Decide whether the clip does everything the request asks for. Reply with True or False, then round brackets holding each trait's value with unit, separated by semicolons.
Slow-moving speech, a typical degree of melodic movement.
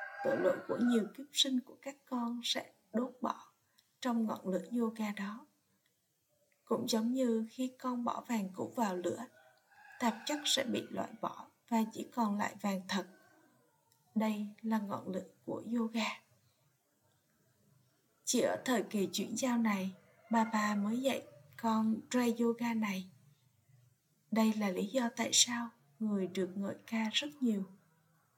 True (150 wpm; 3.6 semitones)